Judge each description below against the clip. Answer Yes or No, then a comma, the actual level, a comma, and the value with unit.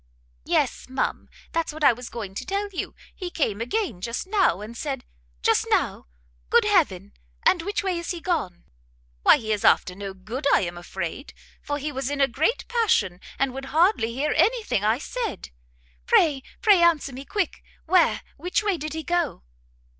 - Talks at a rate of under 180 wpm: No, average, 185 wpm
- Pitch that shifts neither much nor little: No, wide, 7.7 semitones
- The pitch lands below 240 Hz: No, very high, 290 Hz